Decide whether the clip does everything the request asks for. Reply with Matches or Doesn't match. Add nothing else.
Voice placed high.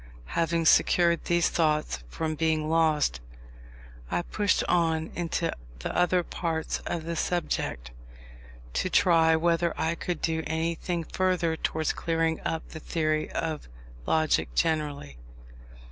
Doesn't match